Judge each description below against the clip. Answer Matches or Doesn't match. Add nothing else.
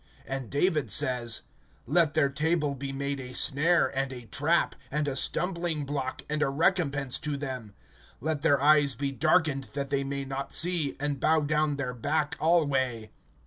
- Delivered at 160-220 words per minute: Matches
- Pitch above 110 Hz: Matches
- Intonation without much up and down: Matches